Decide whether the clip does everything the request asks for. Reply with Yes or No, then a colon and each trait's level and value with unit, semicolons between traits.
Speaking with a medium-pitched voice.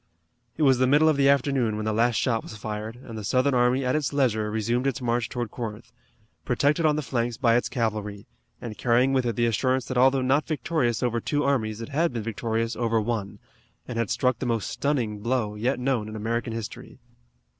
No: low, 120 Hz